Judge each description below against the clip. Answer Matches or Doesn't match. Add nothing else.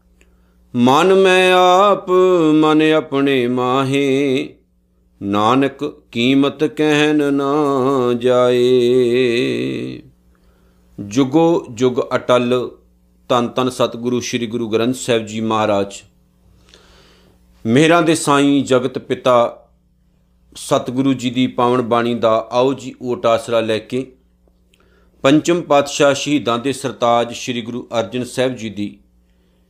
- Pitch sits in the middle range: Doesn't match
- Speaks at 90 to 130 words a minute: Matches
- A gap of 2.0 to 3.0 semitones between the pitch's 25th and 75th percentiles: Doesn't match